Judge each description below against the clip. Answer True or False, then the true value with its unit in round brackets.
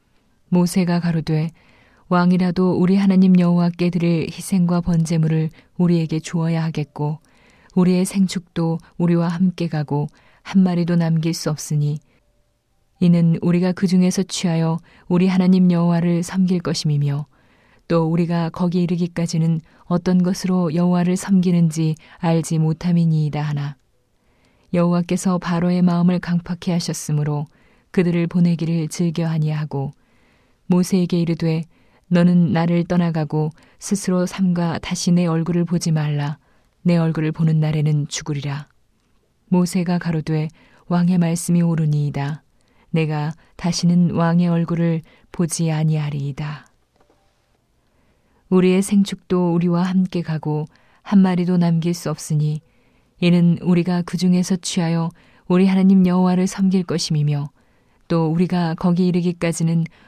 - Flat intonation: True (2.2 semitones)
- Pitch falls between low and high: True (170 Hz)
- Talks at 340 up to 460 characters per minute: False (295 characters per minute)